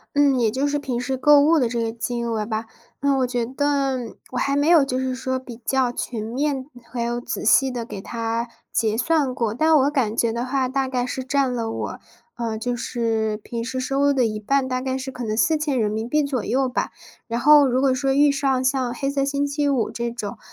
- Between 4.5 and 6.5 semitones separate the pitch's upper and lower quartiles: No, average, 2.9 semitones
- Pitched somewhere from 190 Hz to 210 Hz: No, very high, 255 Hz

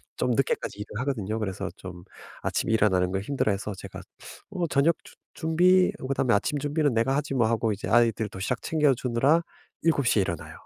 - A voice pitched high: No, low, 120 Hz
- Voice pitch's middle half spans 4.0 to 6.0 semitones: Yes, wide, 5.6 semitones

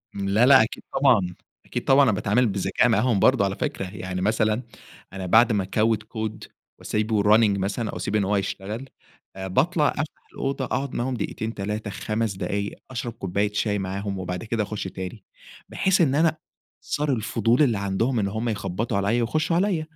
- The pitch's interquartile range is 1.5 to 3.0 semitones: No, average, 3.7 semitones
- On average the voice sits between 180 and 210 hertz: No, low, 110 Hz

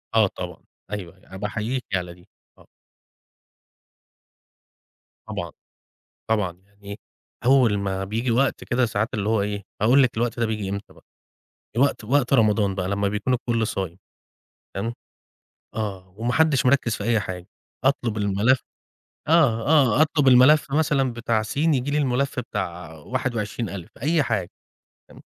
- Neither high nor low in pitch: No, low, 110 Hz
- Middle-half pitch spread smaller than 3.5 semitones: No, average, 4.3 semitones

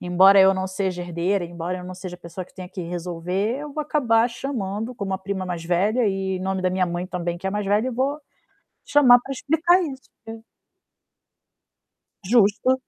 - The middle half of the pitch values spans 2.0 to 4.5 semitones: No, average, 5.0 semitones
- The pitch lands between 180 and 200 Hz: Yes, high, 195 Hz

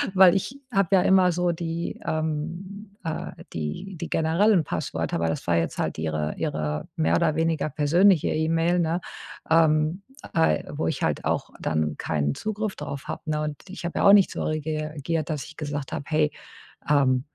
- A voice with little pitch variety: No, average, 3.9 semitones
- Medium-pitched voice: Yes, medium, 155 Hz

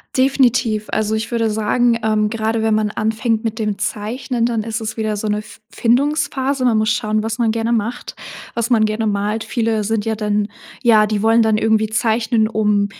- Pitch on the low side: No, high, 220 Hz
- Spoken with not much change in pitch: Yes, narrow, 1.4 semitones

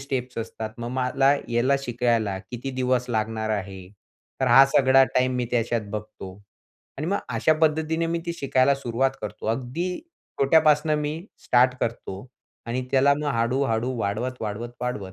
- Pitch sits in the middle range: No, low, 125 Hz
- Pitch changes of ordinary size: Yes, average, 3.3 semitones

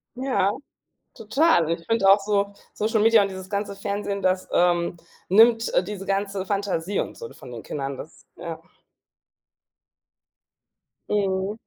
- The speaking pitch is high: Yes, high, 200 Hz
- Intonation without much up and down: Yes, narrow, 2.2 semitones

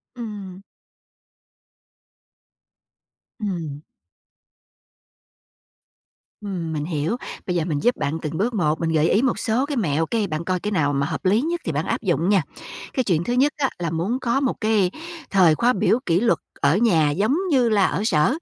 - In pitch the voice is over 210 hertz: No, medium, 185 Hz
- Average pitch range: No, wide, 6.4 semitones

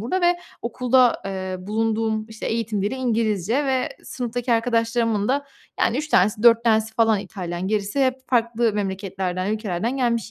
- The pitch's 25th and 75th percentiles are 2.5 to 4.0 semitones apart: Yes, average, 2.9 semitones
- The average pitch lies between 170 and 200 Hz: No, high, 225 Hz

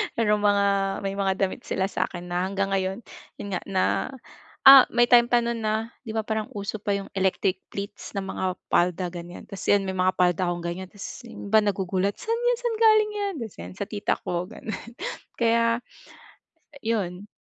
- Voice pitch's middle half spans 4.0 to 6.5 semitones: No, average, 3.5 semitones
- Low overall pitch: No, high, 200 Hz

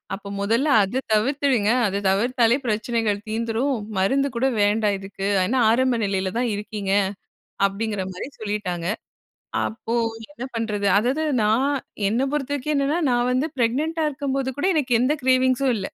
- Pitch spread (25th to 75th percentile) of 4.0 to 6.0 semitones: Yes, average, 4.5 semitones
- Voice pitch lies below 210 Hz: No, high, 235 Hz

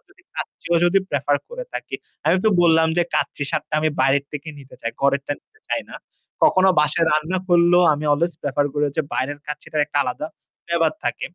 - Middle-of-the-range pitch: Yes, medium, 155 Hz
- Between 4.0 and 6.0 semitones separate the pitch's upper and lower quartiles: No, average, 3.0 semitones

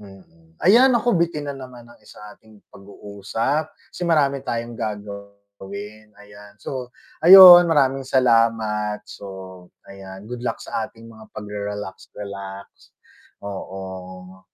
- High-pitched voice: No, low, 105 Hz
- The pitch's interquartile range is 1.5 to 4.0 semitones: No, average, 4.6 semitones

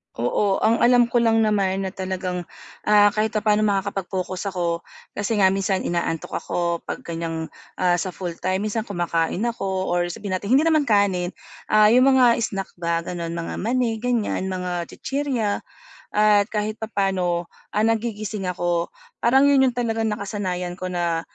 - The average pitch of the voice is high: Yes, high, 200 Hz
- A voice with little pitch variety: No, average, 3.7 semitones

